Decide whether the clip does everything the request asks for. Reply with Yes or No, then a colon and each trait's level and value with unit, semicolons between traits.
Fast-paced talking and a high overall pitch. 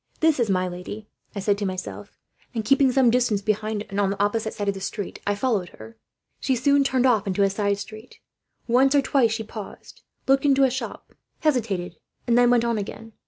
Yes: fast, 210 wpm; high, 220 Hz